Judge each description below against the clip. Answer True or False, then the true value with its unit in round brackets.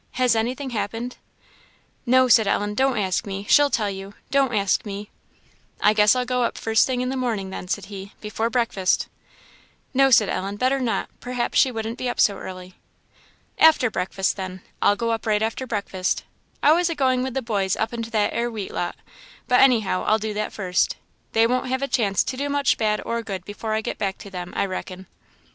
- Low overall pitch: False (220 Hz)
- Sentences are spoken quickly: True (210 wpm)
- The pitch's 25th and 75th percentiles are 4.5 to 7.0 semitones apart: False (4.0 semitones)